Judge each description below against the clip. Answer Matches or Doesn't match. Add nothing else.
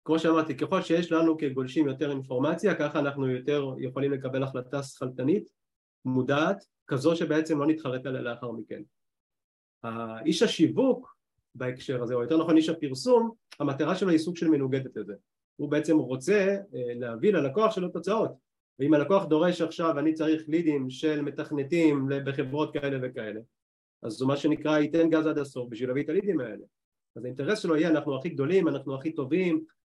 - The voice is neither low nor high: Matches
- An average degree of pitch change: Matches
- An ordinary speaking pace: Doesn't match